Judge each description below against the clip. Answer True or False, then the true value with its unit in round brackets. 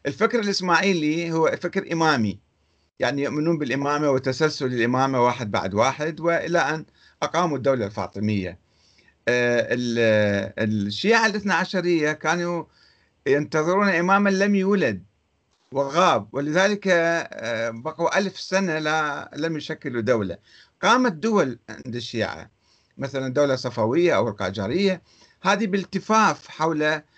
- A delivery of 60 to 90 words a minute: False (110 wpm)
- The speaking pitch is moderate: True (150 Hz)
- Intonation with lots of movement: True (6.7 semitones)